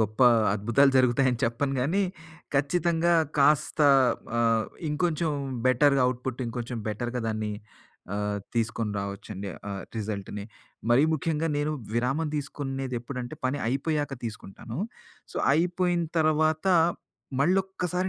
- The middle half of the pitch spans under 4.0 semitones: No, wide, 5.4 semitones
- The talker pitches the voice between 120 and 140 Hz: Yes, low, 135 Hz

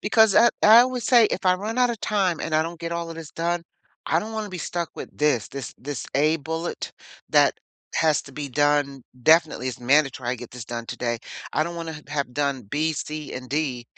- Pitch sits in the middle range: Yes, medium, 155 Hz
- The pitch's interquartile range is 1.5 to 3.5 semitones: No, average, 3.9 semitones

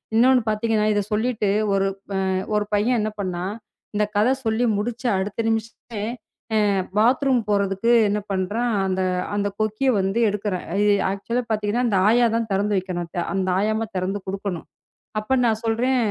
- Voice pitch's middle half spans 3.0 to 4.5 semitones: No, narrow, 2.6 semitones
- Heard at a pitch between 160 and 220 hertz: Yes, high, 210 Hz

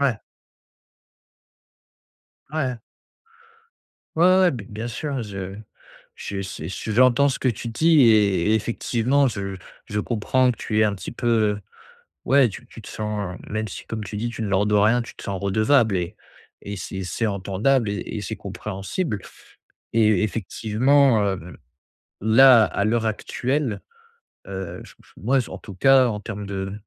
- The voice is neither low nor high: No, low, 110 Hz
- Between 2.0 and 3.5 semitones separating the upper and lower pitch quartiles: No, average, 4.0 semitones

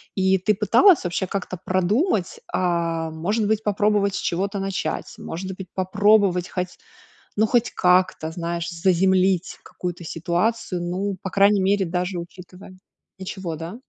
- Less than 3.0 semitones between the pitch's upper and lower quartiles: Yes, narrow, 2.4 semitones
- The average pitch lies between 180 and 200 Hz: Yes, medium, 185 Hz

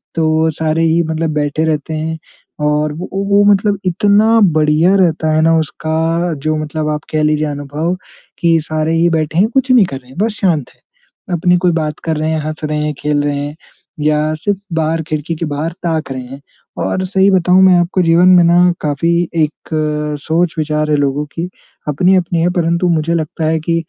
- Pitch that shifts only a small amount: Yes, narrow, 2.2 semitones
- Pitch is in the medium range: Yes, medium, 160 Hz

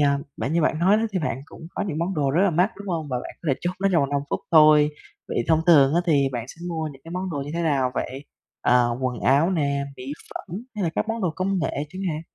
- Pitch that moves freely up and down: No, average, 4.0 semitones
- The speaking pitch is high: No, medium, 155 Hz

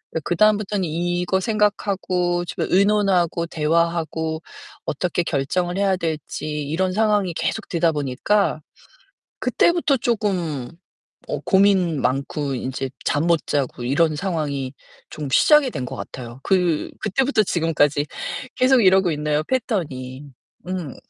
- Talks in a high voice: No, medium, 175 Hz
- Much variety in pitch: No, average, 4.8 semitones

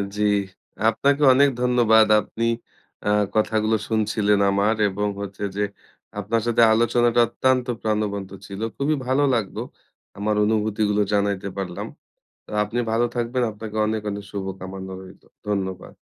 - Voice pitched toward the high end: No, low, 110 Hz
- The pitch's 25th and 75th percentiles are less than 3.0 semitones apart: Yes, narrow, 2.5 semitones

